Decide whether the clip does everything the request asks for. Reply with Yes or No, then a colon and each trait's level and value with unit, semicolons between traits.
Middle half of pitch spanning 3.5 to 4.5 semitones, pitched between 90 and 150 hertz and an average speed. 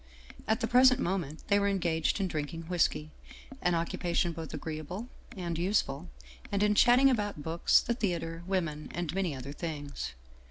No: average, 4.1 semitones; medium, 175 Hz; average, 165 wpm